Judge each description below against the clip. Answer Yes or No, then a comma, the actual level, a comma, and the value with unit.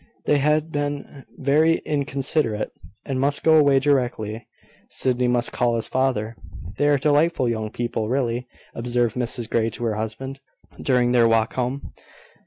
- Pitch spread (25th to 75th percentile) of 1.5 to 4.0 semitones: Yes, average, 3.5 semitones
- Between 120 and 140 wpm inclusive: No, average, 150 wpm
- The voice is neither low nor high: No, low, 125 Hz